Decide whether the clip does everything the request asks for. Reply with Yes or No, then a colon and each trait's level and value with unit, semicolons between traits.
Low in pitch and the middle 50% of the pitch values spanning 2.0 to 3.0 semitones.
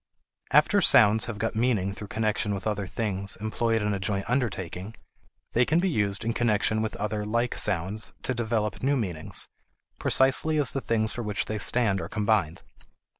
Yes: low, 110 Hz; narrow, 2.6 semitones